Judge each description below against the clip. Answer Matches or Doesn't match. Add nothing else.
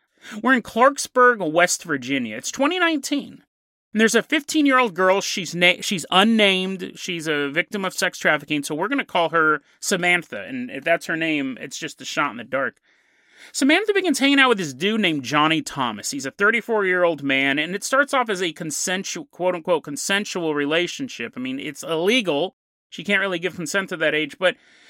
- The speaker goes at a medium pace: Matches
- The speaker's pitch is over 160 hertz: Matches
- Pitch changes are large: Matches